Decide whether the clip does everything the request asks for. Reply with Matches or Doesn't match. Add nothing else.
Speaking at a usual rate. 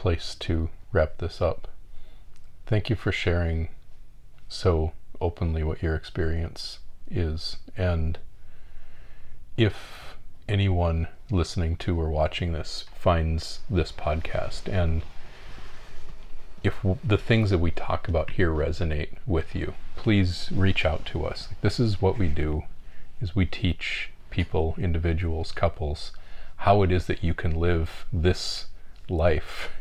Doesn't match